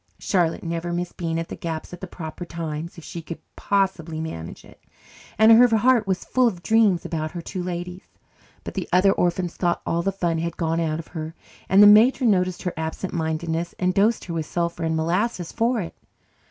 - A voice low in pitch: No, medium, 175 Hz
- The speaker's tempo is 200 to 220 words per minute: Yes, fast, 205 wpm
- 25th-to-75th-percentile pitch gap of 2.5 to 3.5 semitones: Yes, average, 2.8 semitones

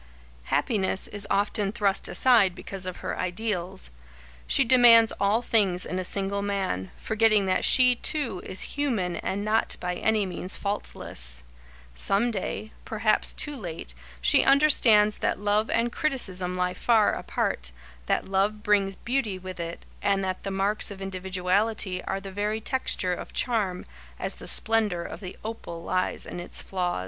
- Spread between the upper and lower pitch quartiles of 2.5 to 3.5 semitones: Yes, average, 3.2 semitones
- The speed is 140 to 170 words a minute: Yes, average, 155 wpm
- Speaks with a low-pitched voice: No, high, 200 Hz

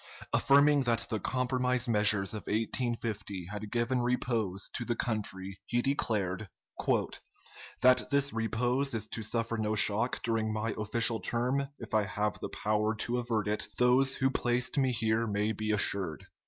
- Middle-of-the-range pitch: No, low, 115 Hz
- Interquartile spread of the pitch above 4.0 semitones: No, average, 2.7 semitones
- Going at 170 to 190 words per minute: No, average, 155 wpm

